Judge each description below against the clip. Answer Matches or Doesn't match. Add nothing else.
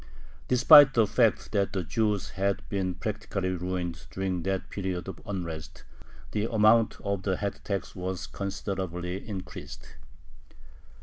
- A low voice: Matches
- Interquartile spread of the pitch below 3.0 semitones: Matches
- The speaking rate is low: Matches